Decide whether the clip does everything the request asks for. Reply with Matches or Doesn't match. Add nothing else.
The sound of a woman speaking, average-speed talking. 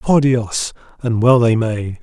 Doesn't match